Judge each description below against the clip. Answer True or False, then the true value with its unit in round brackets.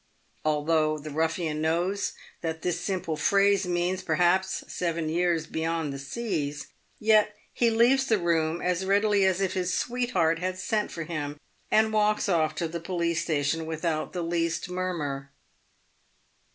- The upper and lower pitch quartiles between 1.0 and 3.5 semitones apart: True (3.1 semitones)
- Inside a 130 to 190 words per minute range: True (150 wpm)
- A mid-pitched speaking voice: True (170 Hz)